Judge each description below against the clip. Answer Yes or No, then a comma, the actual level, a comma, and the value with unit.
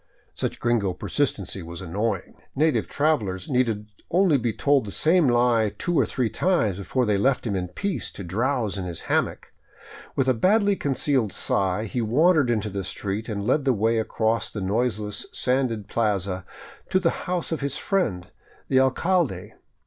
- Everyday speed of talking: Yes, average, 170 wpm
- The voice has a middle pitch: No, low, 115 Hz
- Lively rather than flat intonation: Yes, wide, 5.9 semitones